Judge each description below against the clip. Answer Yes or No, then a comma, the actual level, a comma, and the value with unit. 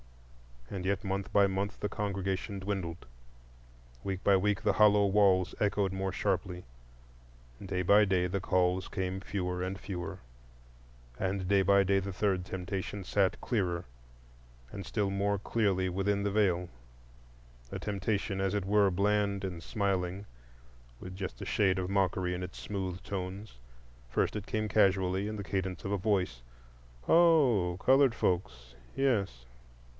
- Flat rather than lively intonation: Yes, narrow, 1.8 semitones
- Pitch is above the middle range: No, very low, 95 Hz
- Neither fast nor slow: Yes, average, 150 wpm